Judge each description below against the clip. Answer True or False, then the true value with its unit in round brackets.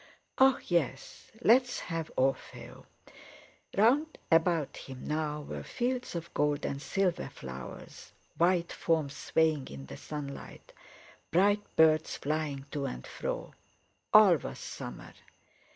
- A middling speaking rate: False (120 wpm)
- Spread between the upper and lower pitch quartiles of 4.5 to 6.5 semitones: True (4.9 semitones)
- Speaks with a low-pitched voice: False (160 Hz)